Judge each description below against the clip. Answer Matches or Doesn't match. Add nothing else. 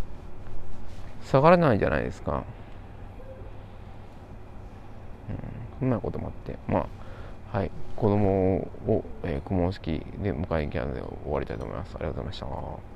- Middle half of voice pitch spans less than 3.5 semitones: Matches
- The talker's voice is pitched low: Matches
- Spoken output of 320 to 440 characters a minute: Doesn't match